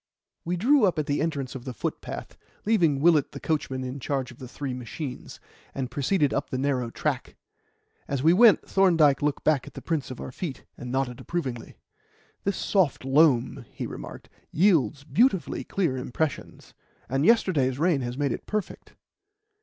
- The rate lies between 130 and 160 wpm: No, average, 170 wpm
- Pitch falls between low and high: Yes, medium, 145 Hz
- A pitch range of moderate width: Yes, average, 4.7 semitones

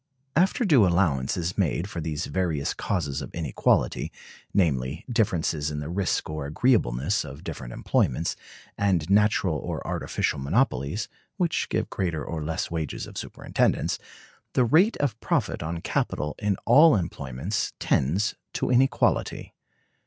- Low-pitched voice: Yes, very low, 85 Hz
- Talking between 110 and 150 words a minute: Yes, average, 140 wpm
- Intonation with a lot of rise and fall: Yes, wide, 5.9 semitones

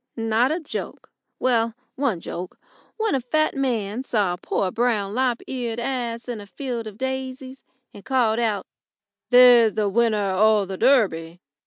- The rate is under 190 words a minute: Yes, average, 160 wpm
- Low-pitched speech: No, high, 235 Hz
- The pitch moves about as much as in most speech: Yes, average, 3.7 semitones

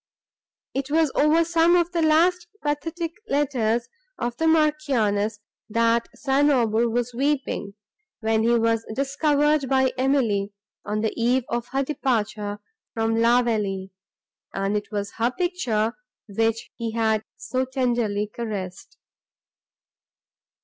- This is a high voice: Yes, high, 240 Hz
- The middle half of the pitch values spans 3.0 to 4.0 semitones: No, average, 4.8 semitones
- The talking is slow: Yes, slow, 125 wpm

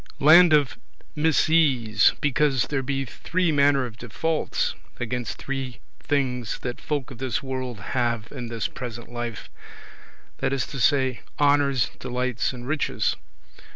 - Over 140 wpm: No, slow, 135 wpm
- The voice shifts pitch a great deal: No, average, 3.0 semitones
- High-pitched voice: No, low, 130 Hz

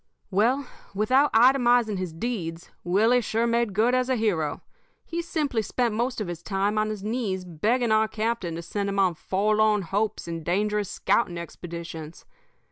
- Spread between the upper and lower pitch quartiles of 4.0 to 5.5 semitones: Yes, average, 4.4 semitones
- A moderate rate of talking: Yes, average, 165 wpm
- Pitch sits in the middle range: No, high, 215 Hz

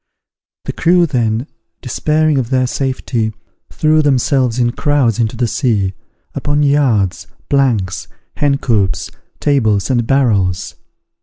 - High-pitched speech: No, low, 125 Hz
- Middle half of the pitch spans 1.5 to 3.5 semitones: No, average, 4.5 semitones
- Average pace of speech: No, slow, 120 wpm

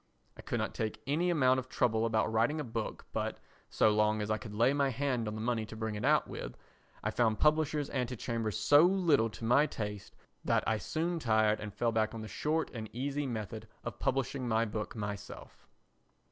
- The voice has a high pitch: No, low, 115 Hz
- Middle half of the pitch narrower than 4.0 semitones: No, average, 4.4 semitones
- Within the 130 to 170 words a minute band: No, average, 200 wpm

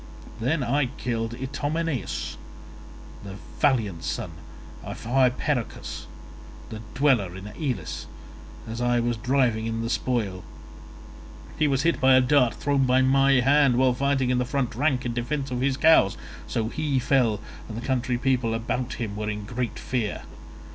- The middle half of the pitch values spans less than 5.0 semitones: Yes, average, 3.0 semitones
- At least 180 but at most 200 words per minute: No, average, 155 wpm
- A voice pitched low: Yes, low, 125 Hz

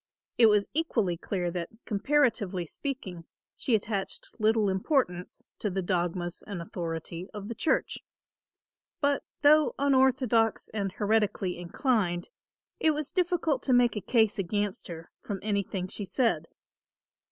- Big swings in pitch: Yes, wide, 5.9 semitones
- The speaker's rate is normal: No, slow, 130 wpm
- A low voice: No, high, 210 Hz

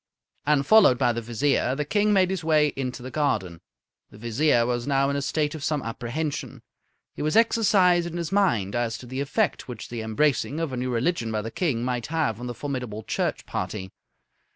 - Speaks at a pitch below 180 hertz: Yes, low, 135 Hz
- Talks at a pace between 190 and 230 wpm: Yes, fast, 205 wpm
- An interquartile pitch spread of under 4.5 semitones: No, average, 5.0 semitones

